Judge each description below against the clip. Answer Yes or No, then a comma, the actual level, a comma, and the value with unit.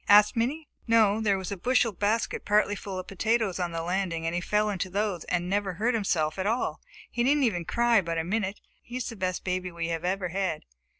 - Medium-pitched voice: No, high, 195 Hz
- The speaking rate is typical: No, fast, 230 wpm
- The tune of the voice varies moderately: Yes, average, 3.7 semitones